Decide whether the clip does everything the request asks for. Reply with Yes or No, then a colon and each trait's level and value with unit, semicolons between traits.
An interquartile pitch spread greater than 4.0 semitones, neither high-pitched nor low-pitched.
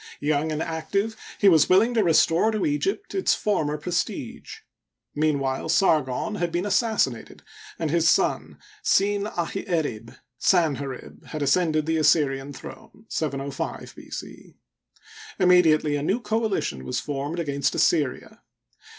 Yes: average, 5.2 semitones; medium, 160 Hz